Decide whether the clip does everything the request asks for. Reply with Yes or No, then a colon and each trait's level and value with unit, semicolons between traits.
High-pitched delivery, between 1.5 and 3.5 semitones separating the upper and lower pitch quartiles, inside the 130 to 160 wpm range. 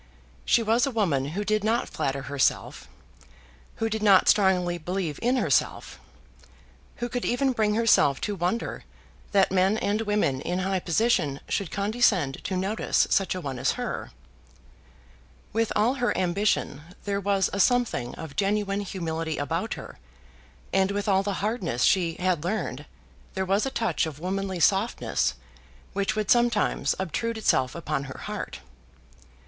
No: high, 195 Hz; average, 4.1 semitones; average, 155 wpm